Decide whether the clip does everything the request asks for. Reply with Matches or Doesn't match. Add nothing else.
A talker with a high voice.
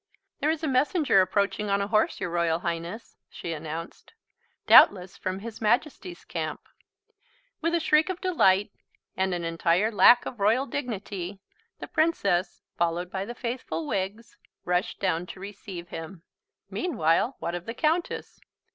Matches